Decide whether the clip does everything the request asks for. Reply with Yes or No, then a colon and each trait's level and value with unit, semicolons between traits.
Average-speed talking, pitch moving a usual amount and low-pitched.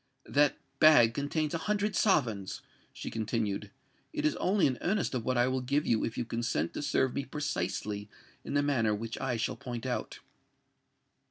Yes: average, 175 wpm; average, 4.7 semitones; low, 130 Hz